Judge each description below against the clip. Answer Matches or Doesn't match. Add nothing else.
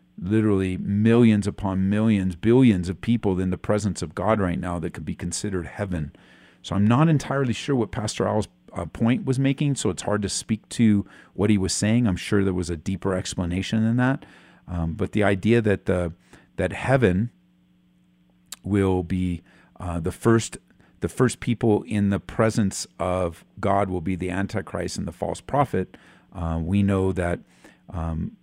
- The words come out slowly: Doesn't match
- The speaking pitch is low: Matches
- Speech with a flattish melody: Doesn't match